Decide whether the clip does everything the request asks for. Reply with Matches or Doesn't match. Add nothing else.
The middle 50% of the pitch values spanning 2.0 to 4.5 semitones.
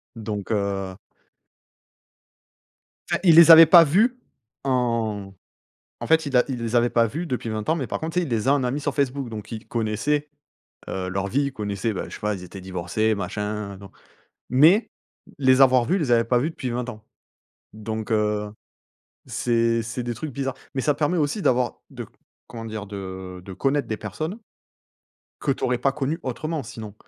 Doesn't match